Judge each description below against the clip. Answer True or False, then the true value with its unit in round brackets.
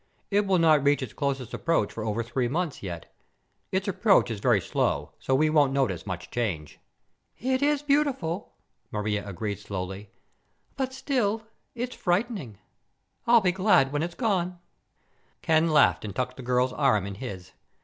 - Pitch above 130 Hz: True (140 Hz)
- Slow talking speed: False (160 wpm)